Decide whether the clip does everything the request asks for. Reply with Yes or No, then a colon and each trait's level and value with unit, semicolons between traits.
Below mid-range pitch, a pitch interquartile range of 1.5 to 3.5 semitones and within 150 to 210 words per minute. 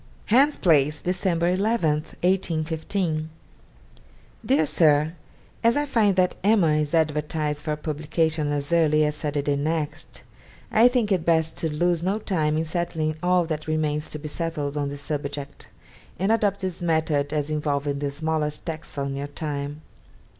No: medium, 155 Hz; average, 2.9 semitones; average, 155 wpm